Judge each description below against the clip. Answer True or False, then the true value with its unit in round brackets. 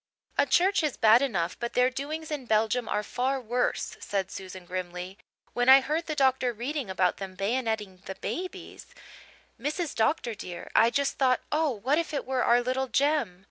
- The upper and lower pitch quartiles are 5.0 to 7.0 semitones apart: True (5.4 semitones)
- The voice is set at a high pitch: True (250 Hz)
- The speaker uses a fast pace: False (180 wpm)